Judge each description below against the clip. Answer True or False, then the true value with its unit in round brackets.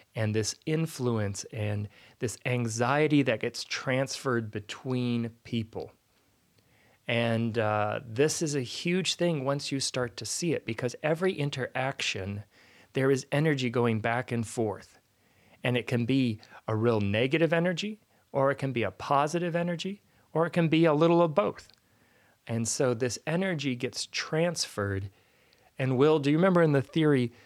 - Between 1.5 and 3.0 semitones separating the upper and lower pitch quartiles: False (5.1 semitones)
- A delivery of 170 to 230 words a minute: False (155 wpm)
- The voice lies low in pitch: True (125 Hz)